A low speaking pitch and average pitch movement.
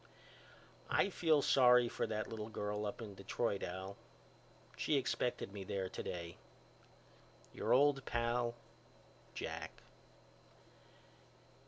Yes: low, 115 Hz; average, 3.8 semitones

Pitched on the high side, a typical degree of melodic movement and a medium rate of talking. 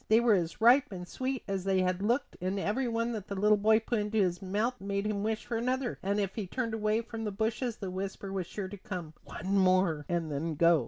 No: high, 205 Hz; average, 3.3 semitones; fast, 250 wpm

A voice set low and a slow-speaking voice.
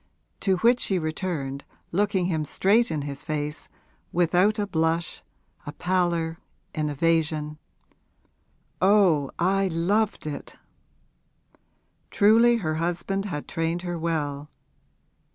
No: medium, 170 Hz; slow, 110 wpm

